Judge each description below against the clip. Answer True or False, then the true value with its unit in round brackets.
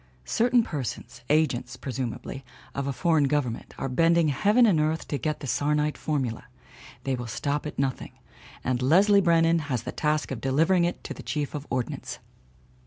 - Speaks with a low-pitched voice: False (150 Hz)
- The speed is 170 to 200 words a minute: True (175 wpm)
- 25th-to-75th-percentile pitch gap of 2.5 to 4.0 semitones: True (3.7 semitones)